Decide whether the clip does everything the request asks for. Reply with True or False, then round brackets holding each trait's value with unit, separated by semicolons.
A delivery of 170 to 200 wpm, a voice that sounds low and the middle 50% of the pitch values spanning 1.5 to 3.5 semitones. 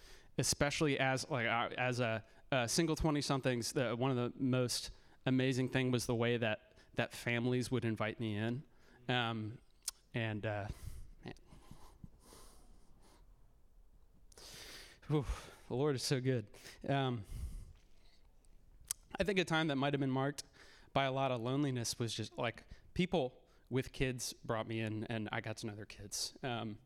False (145 wpm; 125 Hz; 3.1 semitones)